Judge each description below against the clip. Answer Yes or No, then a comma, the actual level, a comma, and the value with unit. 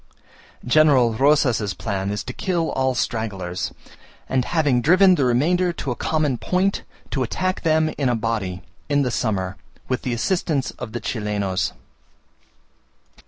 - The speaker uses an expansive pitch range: Yes, wide, 6.1 semitones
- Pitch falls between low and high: No, low, 130 Hz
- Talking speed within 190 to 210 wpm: No, average, 145 wpm